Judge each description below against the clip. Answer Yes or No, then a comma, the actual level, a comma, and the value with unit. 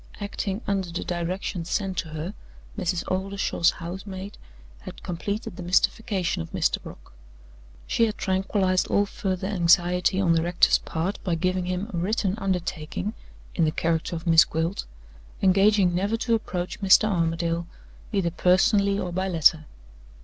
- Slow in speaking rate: No, average, 150 wpm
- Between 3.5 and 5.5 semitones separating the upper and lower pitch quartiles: No, narrow, 2.6 semitones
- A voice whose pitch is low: No, medium, 185 Hz